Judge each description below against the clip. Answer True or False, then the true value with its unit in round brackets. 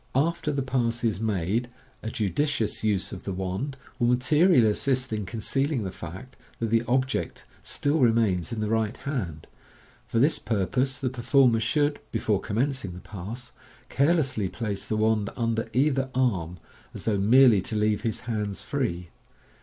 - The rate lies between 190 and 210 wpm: False (165 wpm)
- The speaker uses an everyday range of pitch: True (4.1 semitones)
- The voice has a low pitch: True (115 Hz)